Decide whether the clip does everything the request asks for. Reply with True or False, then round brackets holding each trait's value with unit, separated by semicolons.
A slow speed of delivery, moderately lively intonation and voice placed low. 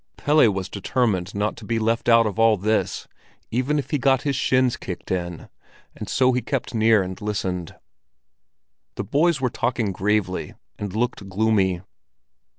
False (155 wpm; 4.6 semitones; 110 Hz)